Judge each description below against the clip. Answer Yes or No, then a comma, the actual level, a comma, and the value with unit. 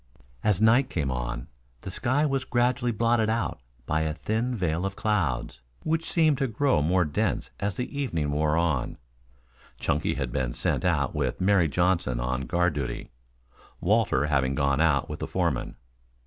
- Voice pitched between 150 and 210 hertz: No, very low, 85 Hz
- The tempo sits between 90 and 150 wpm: No, average, 165 wpm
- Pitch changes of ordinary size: No, wide, 8.5 semitones